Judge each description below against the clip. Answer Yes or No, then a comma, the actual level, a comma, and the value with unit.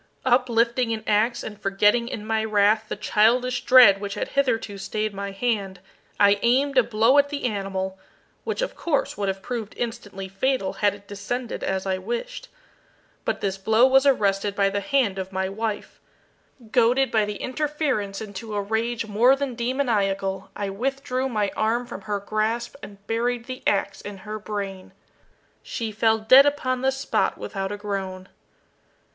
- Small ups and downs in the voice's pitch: No, average, 3.7 semitones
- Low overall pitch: No, high, 215 Hz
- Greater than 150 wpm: Yes, average, 170 wpm